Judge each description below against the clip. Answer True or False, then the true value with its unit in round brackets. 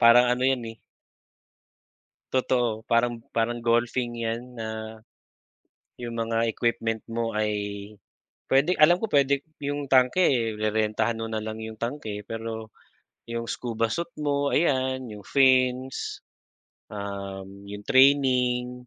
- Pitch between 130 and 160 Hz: False (120 Hz)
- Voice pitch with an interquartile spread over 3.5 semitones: False (2.8 semitones)